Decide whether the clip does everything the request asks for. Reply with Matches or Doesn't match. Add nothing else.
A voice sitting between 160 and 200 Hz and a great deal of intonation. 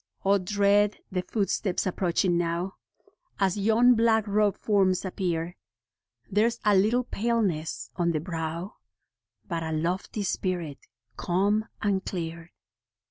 Doesn't match